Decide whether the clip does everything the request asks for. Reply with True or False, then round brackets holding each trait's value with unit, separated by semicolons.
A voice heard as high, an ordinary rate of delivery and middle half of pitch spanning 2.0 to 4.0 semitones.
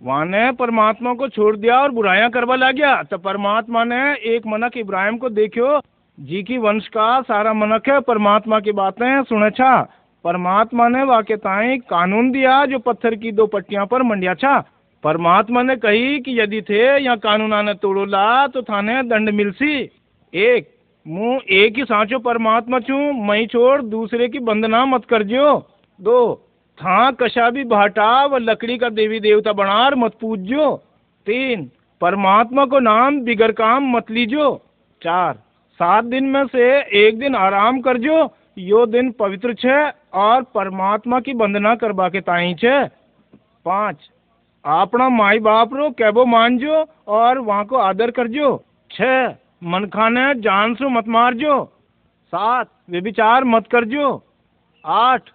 True (235 Hz; 155 wpm; 3.5 semitones)